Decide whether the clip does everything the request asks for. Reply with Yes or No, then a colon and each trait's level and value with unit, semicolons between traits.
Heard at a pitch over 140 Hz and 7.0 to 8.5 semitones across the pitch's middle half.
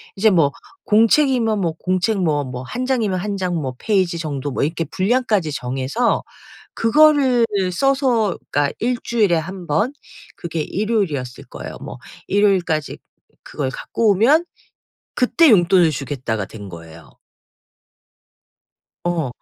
Yes: medium, 185 Hz; wide, 7.6 semitones